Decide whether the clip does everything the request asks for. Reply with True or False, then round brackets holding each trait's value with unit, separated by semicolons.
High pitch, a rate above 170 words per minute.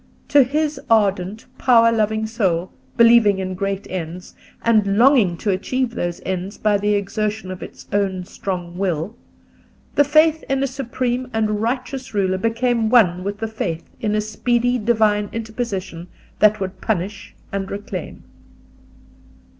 False (210 Hz; 145 wpm)